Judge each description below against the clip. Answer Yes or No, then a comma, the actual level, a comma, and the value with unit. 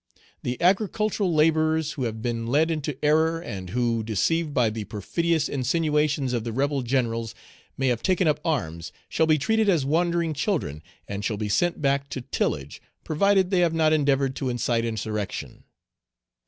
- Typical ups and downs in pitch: No, wide, 5.9 semitones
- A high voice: No, medium, 140 Hz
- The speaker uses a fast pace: No, average, 170 wpm